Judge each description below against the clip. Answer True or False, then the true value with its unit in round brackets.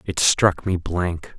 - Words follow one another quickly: False (175 wpm)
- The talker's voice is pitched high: False (90 Hz)